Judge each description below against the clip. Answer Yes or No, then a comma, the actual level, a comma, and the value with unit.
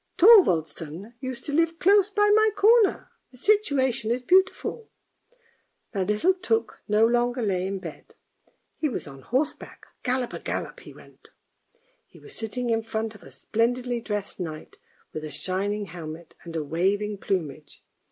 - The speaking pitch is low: No, high, 225 Hz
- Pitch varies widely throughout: Yes, wide, 8.3 semitones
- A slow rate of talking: No, average, 160 wpm